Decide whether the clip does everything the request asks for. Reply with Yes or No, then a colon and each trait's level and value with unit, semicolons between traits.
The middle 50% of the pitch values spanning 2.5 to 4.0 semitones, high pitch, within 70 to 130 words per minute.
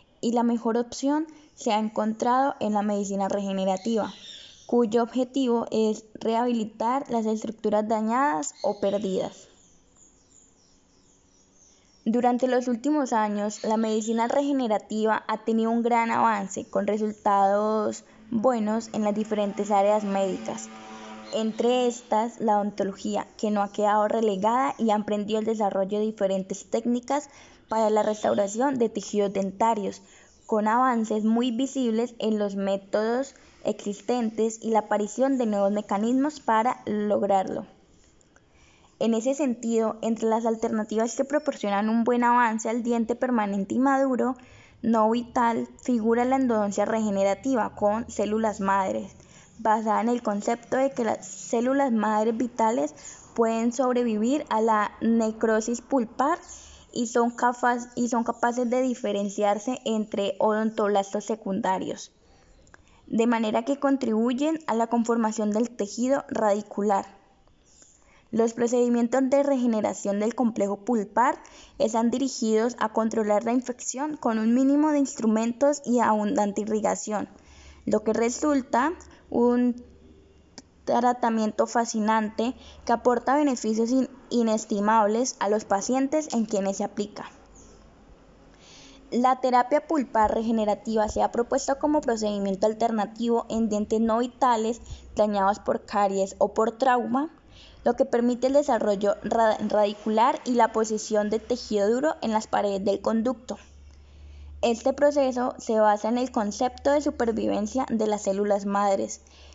Yes: average, 2.9 semitones; high, 225 Hz; slow, 125 wpm